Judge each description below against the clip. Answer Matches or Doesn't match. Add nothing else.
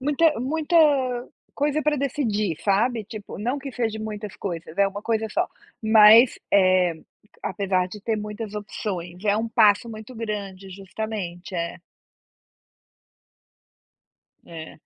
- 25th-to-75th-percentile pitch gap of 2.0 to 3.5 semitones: Matches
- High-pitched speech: Matches